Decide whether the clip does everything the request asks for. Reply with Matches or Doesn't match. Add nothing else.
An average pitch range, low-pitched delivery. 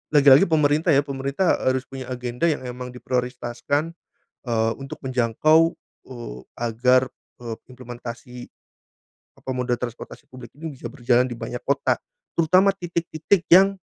Matches